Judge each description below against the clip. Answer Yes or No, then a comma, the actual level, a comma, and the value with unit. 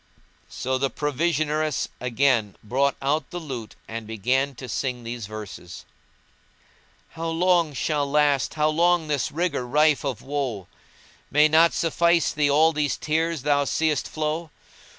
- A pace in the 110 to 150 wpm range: Yes, average, 145 wpm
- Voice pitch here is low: No, medium, 145 Hz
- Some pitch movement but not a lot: Yes, average, 3.7 semitones